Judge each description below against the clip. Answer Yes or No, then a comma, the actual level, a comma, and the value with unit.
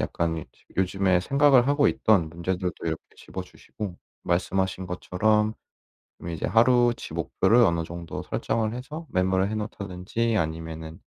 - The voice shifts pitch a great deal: No, average, 4.6 semitones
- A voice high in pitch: No, very low, 95 Hz